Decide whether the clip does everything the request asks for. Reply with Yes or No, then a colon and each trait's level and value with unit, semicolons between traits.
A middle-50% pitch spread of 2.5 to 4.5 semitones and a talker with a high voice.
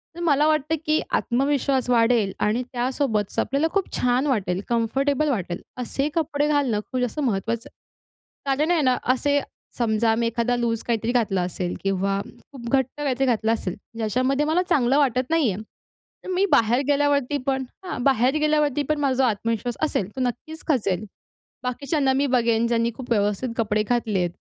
Yes: average, 4.0 semitones; very high, 250 Hz